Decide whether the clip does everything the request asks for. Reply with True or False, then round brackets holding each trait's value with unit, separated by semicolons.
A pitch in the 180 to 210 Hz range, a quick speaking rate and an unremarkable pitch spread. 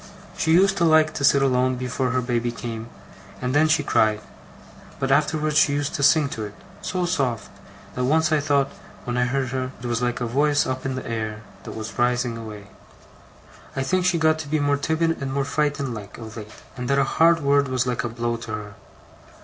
False (135 Hz; 220 wpm; 3.9 semitones)